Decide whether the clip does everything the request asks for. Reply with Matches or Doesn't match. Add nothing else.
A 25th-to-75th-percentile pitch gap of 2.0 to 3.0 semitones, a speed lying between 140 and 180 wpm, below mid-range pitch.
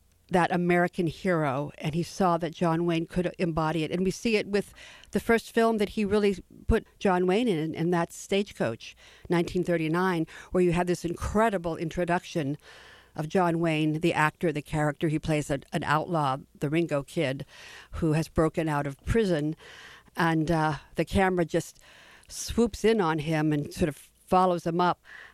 Doesn't match